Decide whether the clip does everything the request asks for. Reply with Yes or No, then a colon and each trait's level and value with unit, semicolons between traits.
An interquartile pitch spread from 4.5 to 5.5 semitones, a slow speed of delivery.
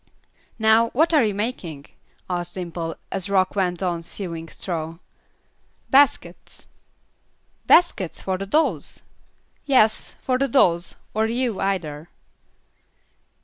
Yes: average, 5.2 semitones; slow, 110 wpm